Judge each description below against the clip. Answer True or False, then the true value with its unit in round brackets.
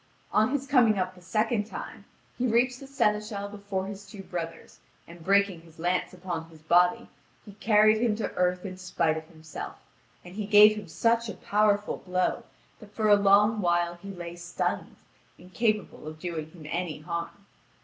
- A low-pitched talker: False (195 Hz)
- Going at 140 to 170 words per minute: False (180 wpm)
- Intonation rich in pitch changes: False (3.5 semitones)